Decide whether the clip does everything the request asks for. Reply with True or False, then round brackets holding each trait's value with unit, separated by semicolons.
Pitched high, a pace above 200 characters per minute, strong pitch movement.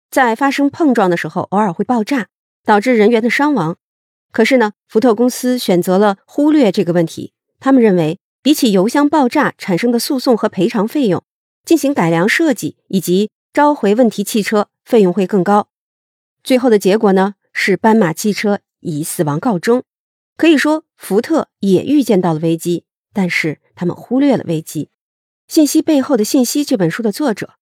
True (215 Hz; 270 characters per minute; 6.1 semitones)